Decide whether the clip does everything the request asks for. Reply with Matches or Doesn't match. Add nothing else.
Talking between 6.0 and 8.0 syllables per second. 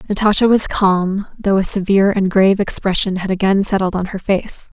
Doesn't match